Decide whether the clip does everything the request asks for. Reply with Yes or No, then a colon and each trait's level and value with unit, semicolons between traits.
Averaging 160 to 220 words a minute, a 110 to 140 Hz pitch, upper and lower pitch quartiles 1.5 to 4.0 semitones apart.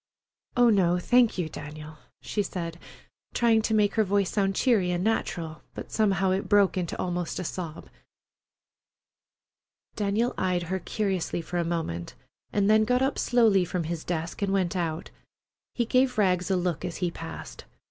No: average, 170 wpm; medium, 185 Hz; average, 3.7 semitones